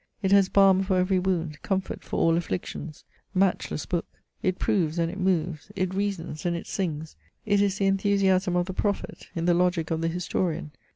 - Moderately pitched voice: Yes, medium, 180 Hz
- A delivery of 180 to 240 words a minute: Yes, average, 190 wpm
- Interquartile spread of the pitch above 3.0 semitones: No, narrow, 2.6 semitones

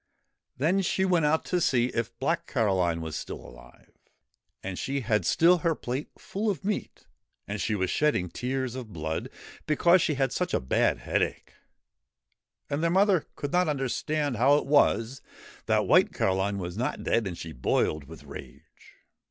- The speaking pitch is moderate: No, low, 130 Hz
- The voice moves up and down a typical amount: No, wide, 8.3 semitones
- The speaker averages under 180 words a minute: Yes, average, 170 wpm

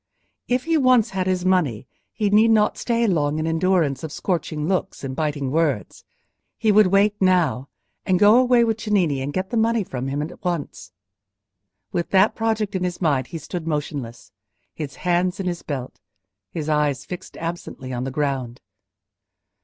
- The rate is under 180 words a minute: Yes, average, 170 wpm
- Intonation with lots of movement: Yes, wide, 6.0 semitones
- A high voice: No, medium, 175 Hz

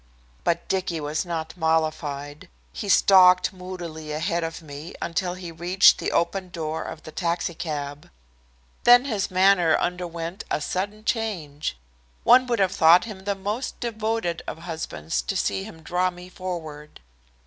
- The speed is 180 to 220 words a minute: No, average, 150 wpm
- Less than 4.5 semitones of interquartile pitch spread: Yes, average, 3.2 semitones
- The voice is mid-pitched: Yes, medium, 175 Hz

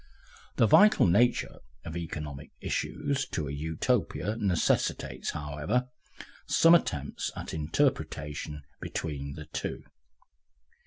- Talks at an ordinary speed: No, slow, 100 wpm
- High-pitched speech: No, very low, 80 Hz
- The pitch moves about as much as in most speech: No, wide, 6.9 semitones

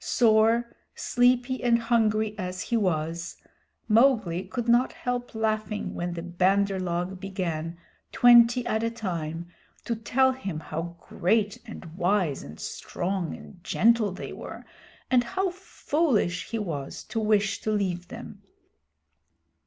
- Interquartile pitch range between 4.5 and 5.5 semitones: Yes, average, 4.8 semitones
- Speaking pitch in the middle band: No, high, 210 Hz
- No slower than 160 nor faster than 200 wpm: No, slow, 135 wpm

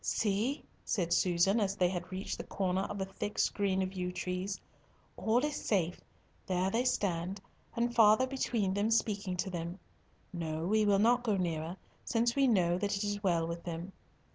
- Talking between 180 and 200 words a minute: Yes, average, 185 wpm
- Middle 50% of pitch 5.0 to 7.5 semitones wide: No, average, 3.1 semitones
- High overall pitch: Yes, high, 195 Hz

